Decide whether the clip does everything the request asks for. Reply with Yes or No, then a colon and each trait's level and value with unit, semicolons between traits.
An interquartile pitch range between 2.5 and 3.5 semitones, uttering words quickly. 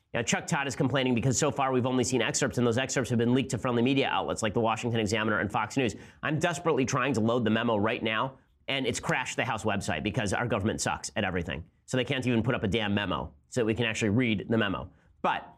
Yes: average, 3.0 semitones; fast, 260 wpm